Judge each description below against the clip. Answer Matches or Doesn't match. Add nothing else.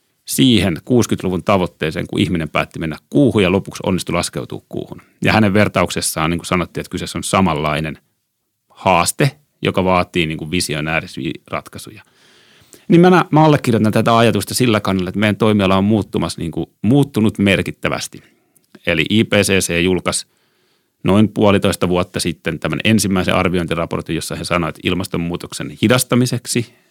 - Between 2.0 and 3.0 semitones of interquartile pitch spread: Doesn't match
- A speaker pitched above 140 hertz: Doesn't match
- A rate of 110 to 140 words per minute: Matches